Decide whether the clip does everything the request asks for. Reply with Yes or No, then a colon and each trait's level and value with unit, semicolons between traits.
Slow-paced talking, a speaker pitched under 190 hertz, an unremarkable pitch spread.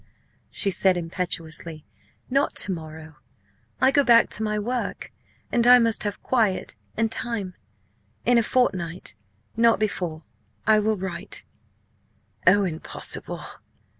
No: slow, 125 wpm; high, 205 Hz; average, 5.0 semitones